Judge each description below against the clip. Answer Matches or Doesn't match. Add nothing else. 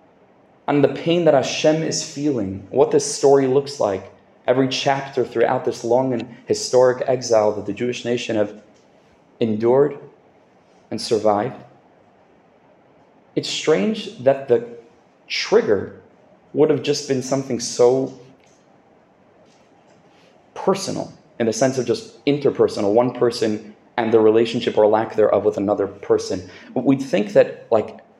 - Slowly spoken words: Matches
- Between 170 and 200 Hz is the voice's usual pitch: Doesn't match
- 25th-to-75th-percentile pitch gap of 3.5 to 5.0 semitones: Matches